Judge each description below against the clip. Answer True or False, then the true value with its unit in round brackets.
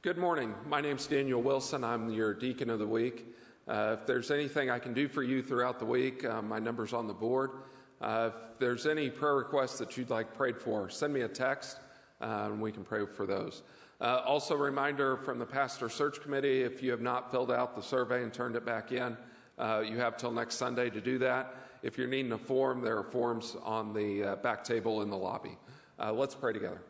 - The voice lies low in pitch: True (125 Hz)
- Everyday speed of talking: False (230 wpm)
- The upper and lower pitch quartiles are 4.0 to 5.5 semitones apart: False (2.7 semitones)